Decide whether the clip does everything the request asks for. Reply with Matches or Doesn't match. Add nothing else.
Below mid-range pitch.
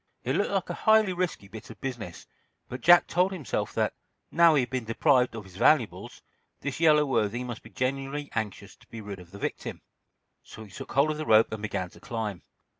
Matches